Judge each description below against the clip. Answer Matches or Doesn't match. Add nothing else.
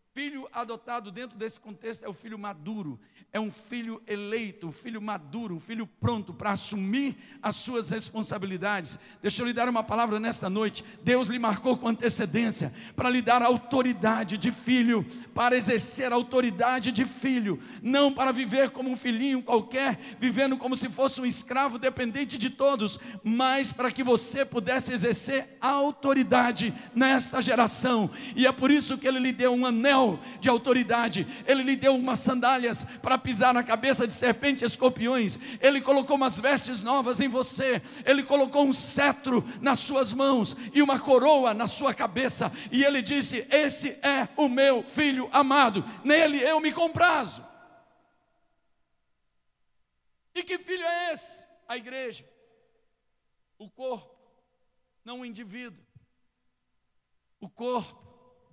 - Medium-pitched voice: Doesn't match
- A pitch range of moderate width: Matches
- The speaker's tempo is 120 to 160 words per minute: Matches